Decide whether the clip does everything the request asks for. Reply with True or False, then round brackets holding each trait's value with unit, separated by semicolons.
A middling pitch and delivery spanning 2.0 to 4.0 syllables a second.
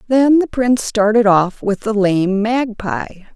False (215 Hz; 3.9 syllables/s)